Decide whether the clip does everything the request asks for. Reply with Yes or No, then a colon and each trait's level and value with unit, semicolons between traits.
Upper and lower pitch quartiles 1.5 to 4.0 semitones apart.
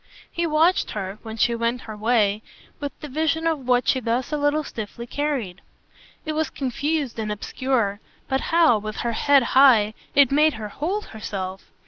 No: wide, 5.4 semitones